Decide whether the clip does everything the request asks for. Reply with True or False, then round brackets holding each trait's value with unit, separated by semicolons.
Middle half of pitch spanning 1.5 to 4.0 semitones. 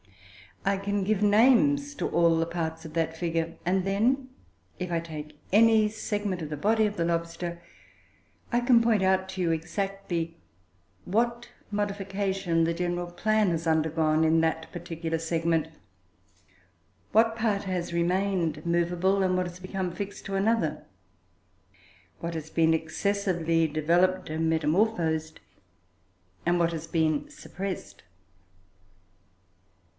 True (3.5 semitones)